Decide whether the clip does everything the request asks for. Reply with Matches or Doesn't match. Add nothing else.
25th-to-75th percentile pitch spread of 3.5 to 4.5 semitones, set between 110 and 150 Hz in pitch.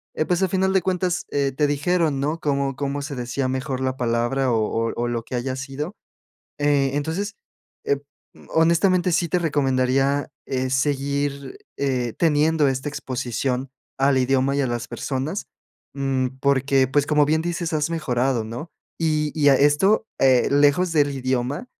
Doesn't match